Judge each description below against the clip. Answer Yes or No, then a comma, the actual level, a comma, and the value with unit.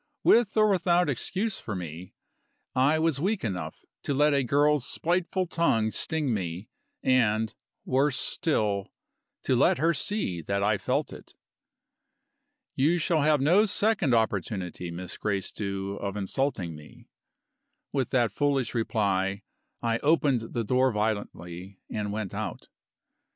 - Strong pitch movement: Yes, wide, 7.3 semitones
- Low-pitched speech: Yes, low, 120 Hz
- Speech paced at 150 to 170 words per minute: No, slow, 135 wpm